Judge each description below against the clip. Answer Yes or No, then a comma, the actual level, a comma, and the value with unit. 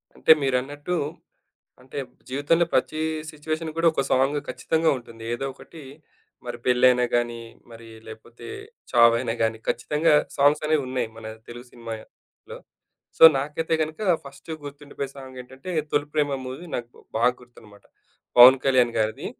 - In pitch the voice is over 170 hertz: No, low, 130 Hz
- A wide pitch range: No, average, 3.7 semitones